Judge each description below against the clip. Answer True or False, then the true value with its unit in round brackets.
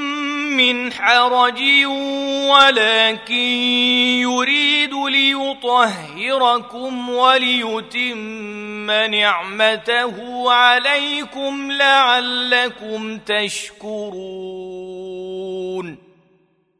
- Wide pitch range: False (3.7 semitones)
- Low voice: False (245 Hz)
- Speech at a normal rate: False (35 wpm)